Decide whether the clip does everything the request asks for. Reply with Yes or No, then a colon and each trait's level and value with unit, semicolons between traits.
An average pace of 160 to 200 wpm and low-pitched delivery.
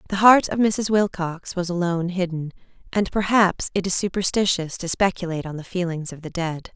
No: average, 185 wpm; medium, 180 Hz